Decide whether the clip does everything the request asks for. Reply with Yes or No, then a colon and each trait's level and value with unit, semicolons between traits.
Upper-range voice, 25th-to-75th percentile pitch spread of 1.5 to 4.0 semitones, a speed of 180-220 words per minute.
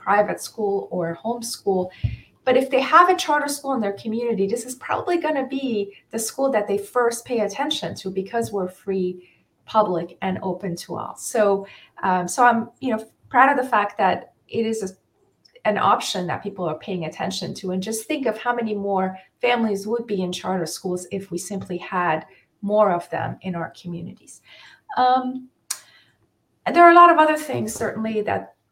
No: high, 205 Hz; average, 4.7 semitones; average, 190 wpm